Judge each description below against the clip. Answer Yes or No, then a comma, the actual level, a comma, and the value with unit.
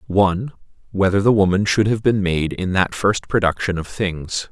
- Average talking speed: Yes, average, 185 wpm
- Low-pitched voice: Yes, very low, 95 Hz